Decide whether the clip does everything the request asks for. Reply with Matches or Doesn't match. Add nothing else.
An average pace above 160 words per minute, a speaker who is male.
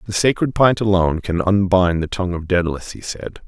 Matches